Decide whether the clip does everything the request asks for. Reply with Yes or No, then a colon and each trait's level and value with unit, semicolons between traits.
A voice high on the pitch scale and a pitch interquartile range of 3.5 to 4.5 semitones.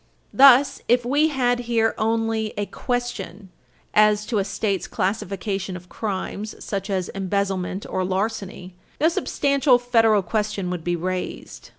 Yes: high, 210 Hz; average, 4.2 semitones